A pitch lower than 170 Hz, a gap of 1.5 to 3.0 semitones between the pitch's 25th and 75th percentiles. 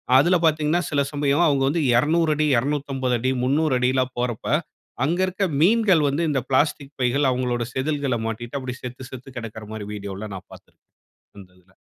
No: low, 135 Hz; average, 3.7 semitones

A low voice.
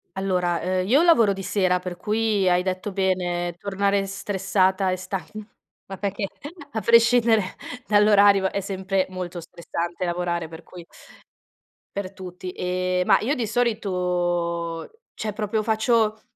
No: high, 190 Hz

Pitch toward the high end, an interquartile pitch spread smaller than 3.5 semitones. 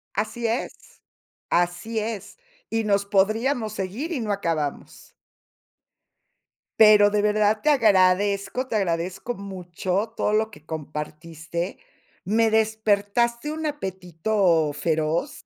No: high, 205 Hz; average, 3.9 semitones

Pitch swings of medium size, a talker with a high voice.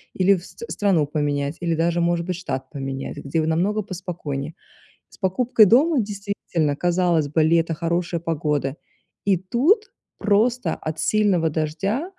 No: average, 4.5 semitones; medium, 170 Hz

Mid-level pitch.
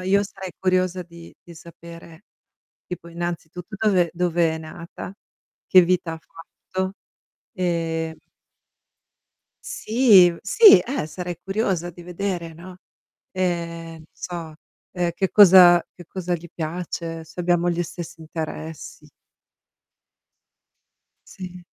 Yes: medium, 175 Hz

